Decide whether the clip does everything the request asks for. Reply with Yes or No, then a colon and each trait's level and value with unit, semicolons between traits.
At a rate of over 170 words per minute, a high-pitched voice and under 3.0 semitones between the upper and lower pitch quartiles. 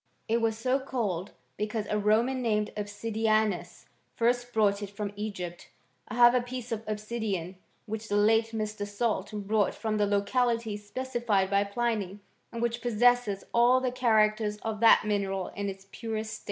No: average, 165 wpm; high, 215 Hz; narrow, 2.5 semitones